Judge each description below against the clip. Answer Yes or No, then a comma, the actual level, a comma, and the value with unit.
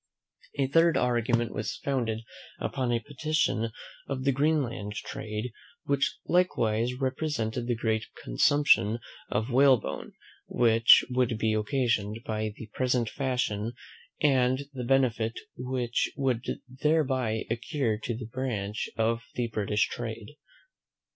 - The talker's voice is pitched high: No, low, 120 Hz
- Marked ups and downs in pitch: No, average, 3.0 semitones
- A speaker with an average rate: No, slow, 120 wpm